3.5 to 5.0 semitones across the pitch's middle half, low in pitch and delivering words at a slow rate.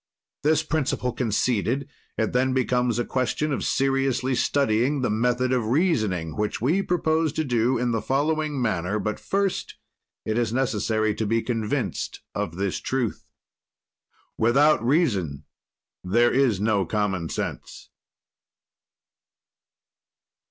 Yes: average, 4.0 semitones; low, 125 Hz; slow, 125 wpm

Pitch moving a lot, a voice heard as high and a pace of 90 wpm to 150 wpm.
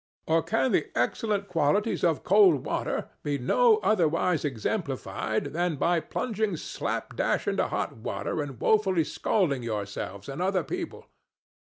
No: wide, 6.3 semitones; medium, 170 Hz; slow, 135 wpm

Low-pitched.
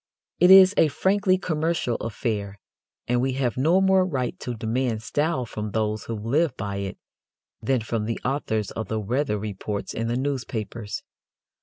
Yes: low, 120 Hz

